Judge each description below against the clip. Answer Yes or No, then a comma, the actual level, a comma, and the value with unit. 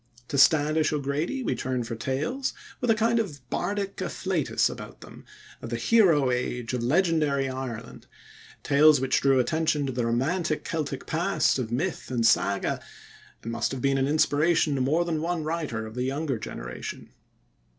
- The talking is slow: No, average, 170 wpm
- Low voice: No, medium, 145 Hz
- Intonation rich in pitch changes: No, average, 4.4 semitones